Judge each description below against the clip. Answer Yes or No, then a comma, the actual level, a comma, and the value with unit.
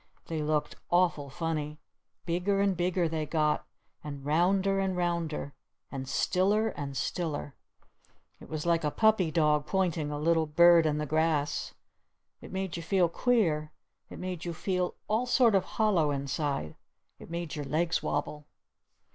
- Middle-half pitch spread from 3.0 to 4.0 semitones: Yes, average, 3.4 semitones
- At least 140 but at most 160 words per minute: Yes, average, 155 wpm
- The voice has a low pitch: No, medium, 165 Hz